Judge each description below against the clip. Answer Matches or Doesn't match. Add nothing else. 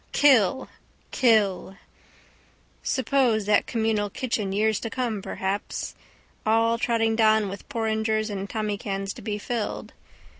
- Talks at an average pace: Doesn't match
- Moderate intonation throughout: Doesn't match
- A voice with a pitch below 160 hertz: Doesn't match